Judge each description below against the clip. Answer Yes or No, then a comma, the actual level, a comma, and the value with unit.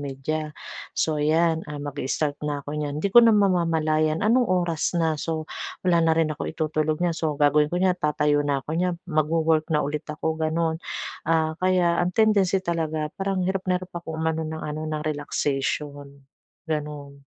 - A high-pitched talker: No, medium, 155 Hz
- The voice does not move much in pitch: Yes, narrow, 2.3 semitones